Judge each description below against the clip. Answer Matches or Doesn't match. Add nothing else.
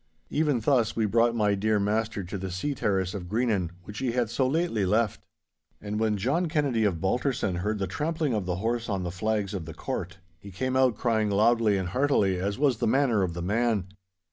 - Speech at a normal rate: Doesn't match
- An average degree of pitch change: Matches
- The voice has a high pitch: Doesn't match